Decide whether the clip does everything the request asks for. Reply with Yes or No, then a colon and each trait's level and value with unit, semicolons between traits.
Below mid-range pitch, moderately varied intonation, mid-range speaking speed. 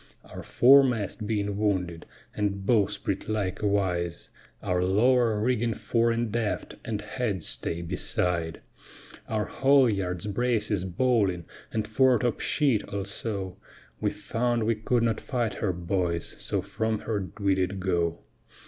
No: low, 105 Hz; average, 3.7 semitones; slow, 120 wpm